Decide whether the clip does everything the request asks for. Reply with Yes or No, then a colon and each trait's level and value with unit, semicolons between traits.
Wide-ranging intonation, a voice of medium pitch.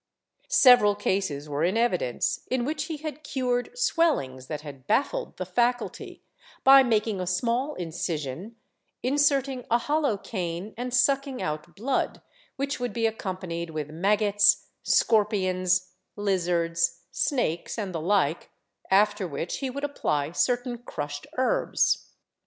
No: wide, 6.9 semitones; high, 210 Hz